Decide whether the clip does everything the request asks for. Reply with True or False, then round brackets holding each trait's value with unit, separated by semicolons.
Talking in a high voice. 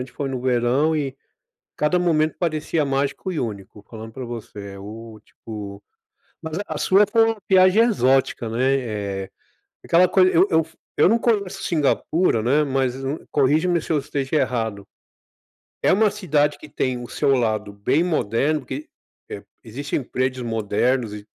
False (135 Hz)